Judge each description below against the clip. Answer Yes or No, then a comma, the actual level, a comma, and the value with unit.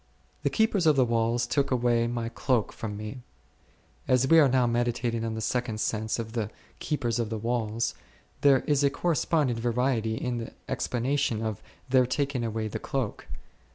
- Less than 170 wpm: No, average, 175 wpm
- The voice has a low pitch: Yes, low, 120 Hz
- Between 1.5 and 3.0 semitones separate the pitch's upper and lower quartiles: Yes, average, 2.7 semitones